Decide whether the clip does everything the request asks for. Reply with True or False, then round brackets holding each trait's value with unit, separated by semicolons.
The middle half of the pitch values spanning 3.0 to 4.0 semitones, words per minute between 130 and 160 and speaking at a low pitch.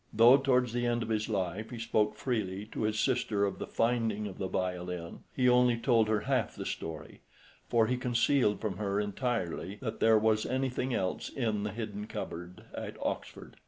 False (3.3 semitones; 190 wpm; 110 Hz)